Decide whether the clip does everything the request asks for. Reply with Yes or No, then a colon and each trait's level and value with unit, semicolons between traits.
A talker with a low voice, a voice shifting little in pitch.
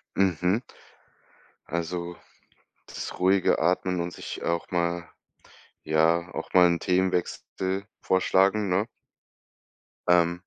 Yes: very low, 90 Hz; narrow, 1.5 semitones